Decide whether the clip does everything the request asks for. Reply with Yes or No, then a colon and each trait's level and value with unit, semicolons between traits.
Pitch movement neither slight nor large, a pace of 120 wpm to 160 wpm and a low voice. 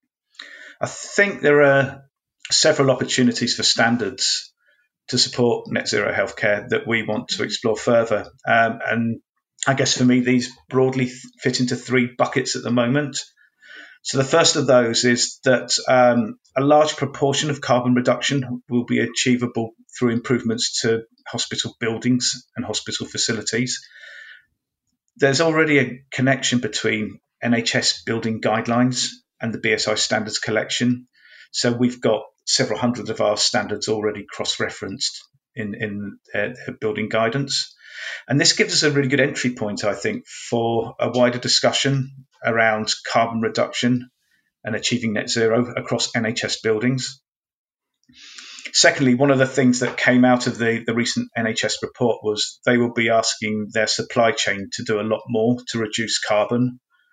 Yes: average, 3.0 semitones; average, 150 wpm; low, 125 Hz